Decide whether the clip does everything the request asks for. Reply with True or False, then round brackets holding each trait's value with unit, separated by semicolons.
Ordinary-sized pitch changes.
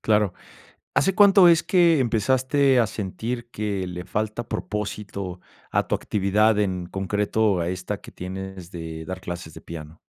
True (4.2 semitones)